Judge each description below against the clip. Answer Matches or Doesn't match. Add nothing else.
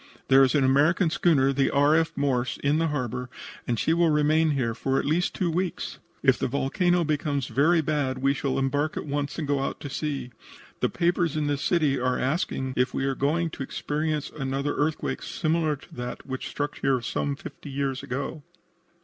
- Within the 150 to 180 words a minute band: Doesn't match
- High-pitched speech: Doesn't match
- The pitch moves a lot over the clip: Doesn't match